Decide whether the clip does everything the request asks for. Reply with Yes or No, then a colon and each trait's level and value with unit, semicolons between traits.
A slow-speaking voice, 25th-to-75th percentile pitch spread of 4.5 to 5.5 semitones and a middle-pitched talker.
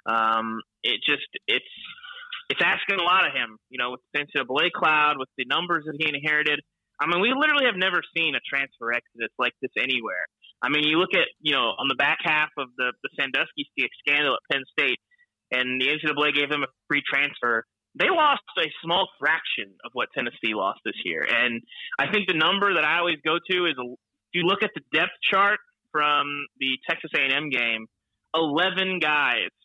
No: average, 200 wpm; average, 4.8 semitones; medium, 150 Hz